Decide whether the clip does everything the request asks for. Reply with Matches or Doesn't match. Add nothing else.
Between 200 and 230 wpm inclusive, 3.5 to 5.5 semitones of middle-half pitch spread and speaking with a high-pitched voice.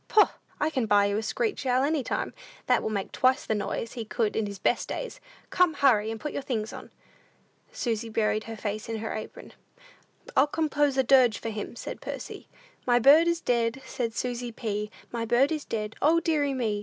Matches